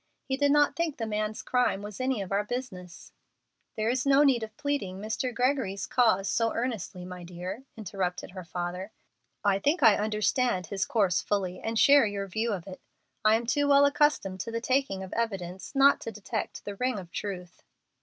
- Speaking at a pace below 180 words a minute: No, average, 195 wpm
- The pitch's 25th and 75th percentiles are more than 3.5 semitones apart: Yes, average, 4.9 semitones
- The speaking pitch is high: Yes, high, 215 Hz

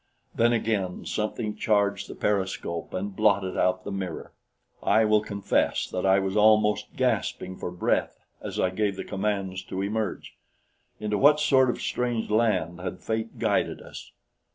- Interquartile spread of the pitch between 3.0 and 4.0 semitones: No, narrow, 2.4 semitones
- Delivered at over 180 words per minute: No, average, 155 wpm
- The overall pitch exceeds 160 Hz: No, low, 100 Hz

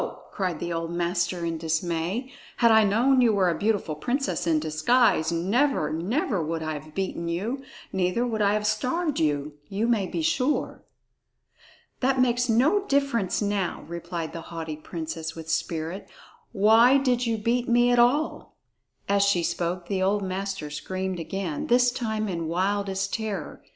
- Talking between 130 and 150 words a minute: No, average, 160 wpm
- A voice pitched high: Yes, high, 195 Hz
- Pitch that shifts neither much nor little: No, wide, 6.0 semitones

